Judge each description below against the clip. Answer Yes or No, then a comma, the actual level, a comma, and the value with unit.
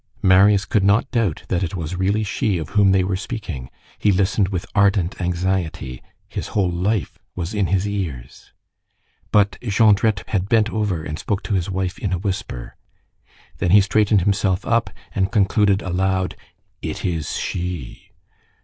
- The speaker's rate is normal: Yes, average, 160 wpm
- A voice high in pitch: No, very low, 95 Hz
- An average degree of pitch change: No, narrow, 2.3 semitones